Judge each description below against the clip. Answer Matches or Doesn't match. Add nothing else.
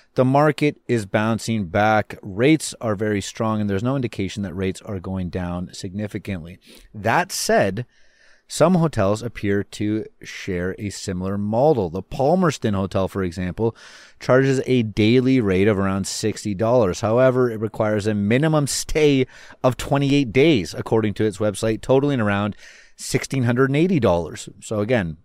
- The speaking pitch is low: Matches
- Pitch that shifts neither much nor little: Matches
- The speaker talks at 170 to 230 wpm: Doesn't match